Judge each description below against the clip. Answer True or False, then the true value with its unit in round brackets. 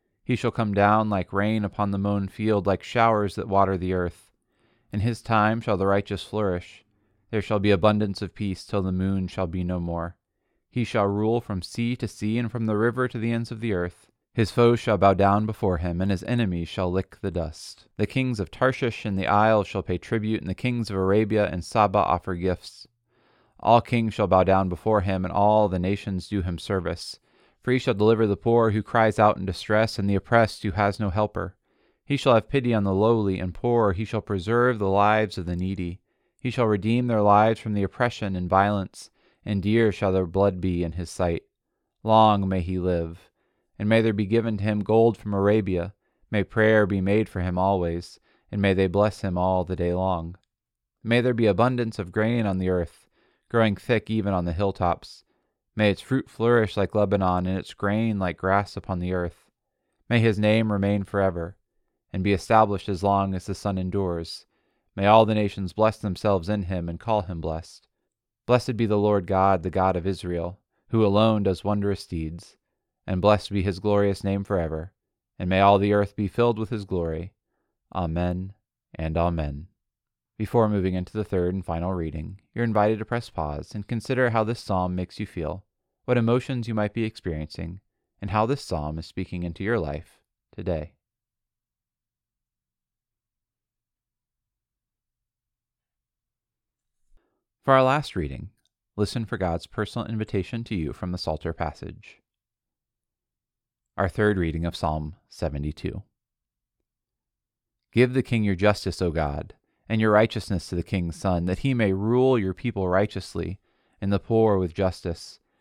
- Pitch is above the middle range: False (100 Hz)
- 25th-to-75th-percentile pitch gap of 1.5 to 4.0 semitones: True (3.3 semitones)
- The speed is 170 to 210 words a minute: True (185 wpm)